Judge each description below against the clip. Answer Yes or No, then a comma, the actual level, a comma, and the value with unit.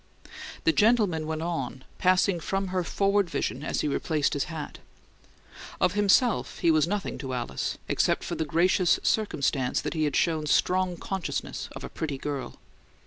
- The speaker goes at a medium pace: Yes, average, 165 wpm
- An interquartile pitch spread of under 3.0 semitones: No, average, 4.4 semitones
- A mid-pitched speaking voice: Yes, medium, 165 Hz